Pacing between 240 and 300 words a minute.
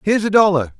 No: fast, 230 wpm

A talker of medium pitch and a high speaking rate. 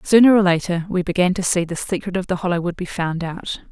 Yes: medium, 180 Hz; fast, 260 wpm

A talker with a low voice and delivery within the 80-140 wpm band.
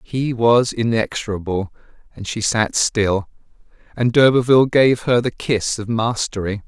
Yes: low, 115 Hz; slow, 135 wpm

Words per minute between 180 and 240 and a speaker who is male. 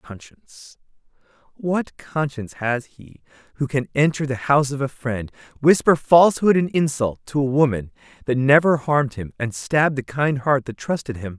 No: average, 170 wpm; male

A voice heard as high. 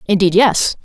Yes: high, 200 Hz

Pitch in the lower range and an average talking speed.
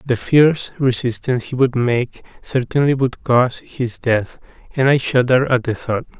Yes: low, 125 Hz; average, 165 wpm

